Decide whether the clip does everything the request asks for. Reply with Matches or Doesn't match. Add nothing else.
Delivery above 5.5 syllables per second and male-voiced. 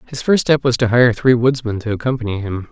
Matches